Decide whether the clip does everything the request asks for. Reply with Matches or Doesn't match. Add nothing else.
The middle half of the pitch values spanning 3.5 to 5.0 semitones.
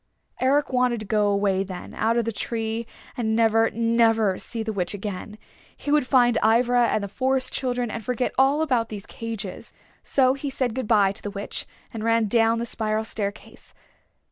Doesn't match